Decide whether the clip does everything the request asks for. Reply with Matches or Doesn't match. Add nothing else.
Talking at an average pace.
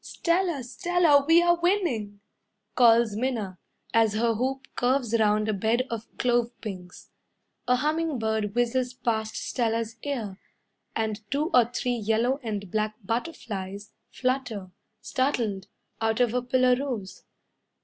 Doesn't match